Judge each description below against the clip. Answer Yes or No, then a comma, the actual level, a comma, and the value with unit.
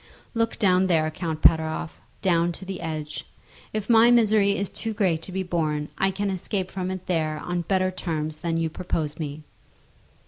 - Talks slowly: No, average, 185 wpm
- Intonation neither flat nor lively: Yes, average, 3.3 semitones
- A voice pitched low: No, medium, 180 Hz